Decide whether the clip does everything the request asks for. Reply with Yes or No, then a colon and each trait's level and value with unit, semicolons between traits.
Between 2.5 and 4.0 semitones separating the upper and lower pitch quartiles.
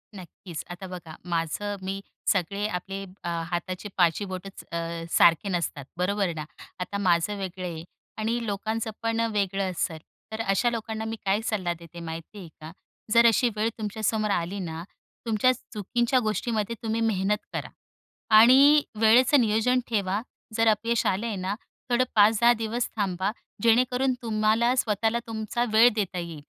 Yes: average, 3.6 semitones